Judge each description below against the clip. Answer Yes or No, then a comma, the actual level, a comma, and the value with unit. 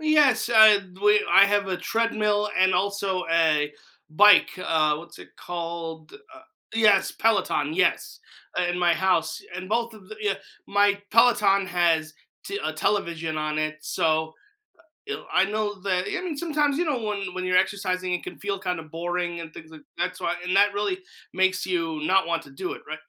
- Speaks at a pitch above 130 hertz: Yes, medium, 185 Hz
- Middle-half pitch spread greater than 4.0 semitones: No, average, 3.7 semitones